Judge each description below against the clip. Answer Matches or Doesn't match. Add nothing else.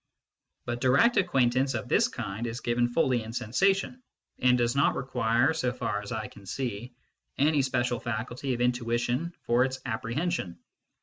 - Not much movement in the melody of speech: Matches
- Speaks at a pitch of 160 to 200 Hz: Doesn't match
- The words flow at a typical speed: Matches